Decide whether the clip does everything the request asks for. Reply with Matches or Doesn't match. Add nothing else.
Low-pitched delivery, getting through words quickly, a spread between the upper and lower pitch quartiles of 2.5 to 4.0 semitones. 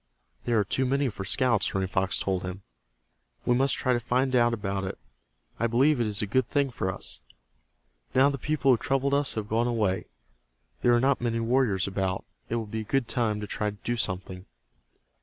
Doesn't match